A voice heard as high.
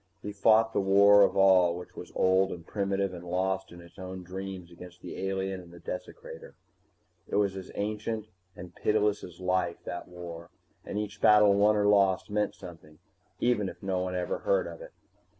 No: very low, 95 Hz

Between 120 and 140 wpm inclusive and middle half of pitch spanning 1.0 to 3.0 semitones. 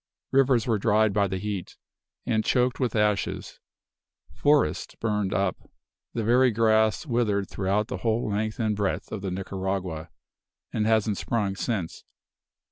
Yes: slow, 135 wpm; narrow, 2.6 semitones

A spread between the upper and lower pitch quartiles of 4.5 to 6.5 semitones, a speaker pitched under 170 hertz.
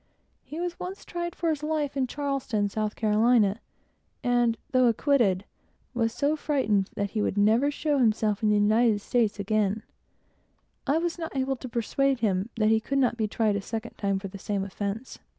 No: average, 4.8 semitones; high, 230 Hz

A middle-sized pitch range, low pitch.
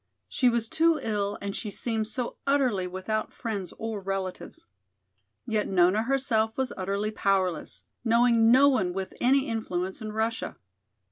No: average, 3.4 semitones; high, 220 Hz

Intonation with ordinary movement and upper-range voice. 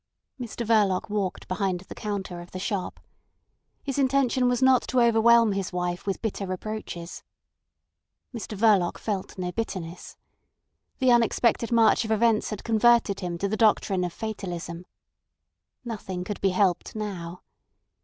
Yes: average, 3.9 semitones; high, 205 Hz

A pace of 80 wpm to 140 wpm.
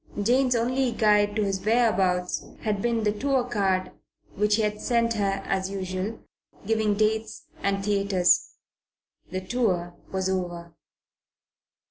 Yes: slow, 135 wpm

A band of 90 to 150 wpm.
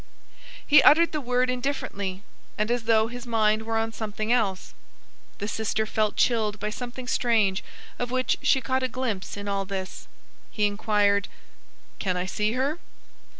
No: average, 160 wpm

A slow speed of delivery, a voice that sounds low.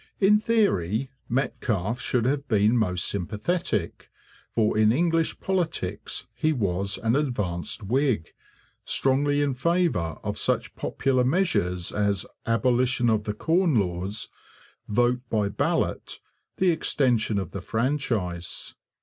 Yes: slow, 120 wpm; low, 120 Hz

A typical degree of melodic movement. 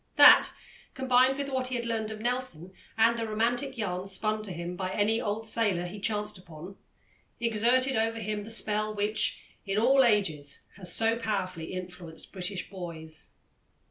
Yes: average, 3.9 semitones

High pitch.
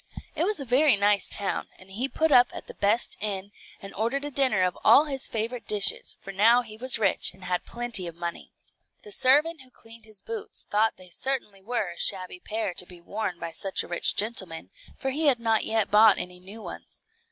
Yes: high, 220 Hz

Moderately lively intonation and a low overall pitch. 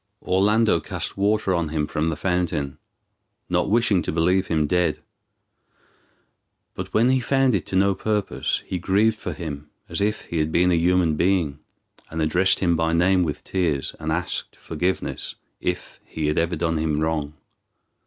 Yes: average, 3.4 semitones; very low, 90 Hz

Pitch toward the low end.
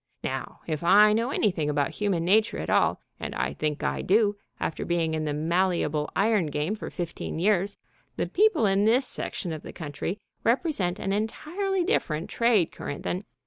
No: high, 190 Hz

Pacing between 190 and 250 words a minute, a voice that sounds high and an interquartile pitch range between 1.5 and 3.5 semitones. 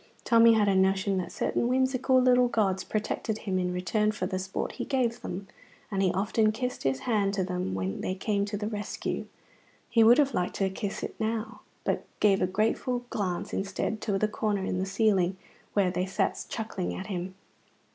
Yes: average, 195 wpm; high, 200 Hz; average, 2.9 semitones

